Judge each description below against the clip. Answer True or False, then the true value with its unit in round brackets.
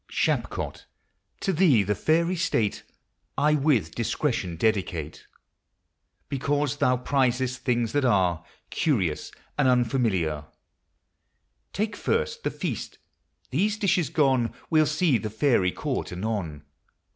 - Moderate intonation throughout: False (6.7 semitones)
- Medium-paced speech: False (110 wpm)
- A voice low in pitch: True (125 Hz)